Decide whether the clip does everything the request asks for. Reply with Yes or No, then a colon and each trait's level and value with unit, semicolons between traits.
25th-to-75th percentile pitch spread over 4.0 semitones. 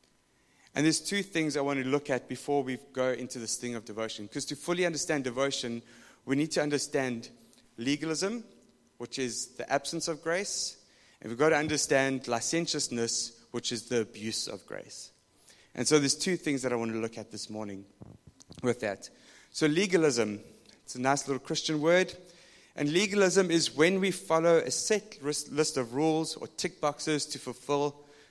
Yes: average, 4.8 semitones